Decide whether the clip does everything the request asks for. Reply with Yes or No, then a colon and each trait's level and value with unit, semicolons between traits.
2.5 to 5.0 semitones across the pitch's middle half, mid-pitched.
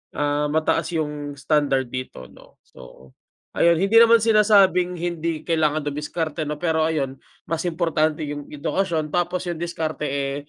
Yes: average, 2.8 semitones; medium, 155 Hz